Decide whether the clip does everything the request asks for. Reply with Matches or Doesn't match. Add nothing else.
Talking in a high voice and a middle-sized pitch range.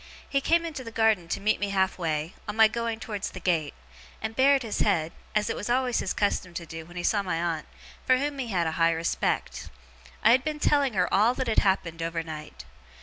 Doesn't match